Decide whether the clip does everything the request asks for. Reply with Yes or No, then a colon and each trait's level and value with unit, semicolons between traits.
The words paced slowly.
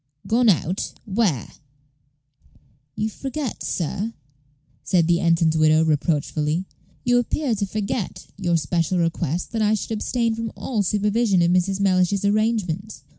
Yes: slow, 130 wpm